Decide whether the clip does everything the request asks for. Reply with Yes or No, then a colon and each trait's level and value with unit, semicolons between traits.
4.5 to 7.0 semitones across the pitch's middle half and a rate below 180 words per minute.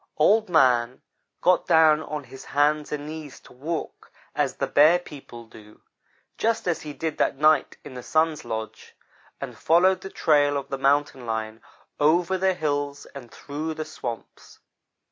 No: average, 3.2 semitones; average, 165 wpm